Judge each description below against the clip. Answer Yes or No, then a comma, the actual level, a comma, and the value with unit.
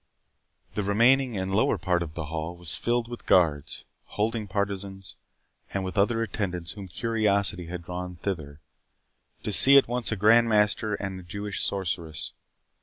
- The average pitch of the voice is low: Yes, low, 100 Hz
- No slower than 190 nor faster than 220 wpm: No, average, 160 wpm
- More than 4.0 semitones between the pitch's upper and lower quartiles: No, average, 3.5 semitones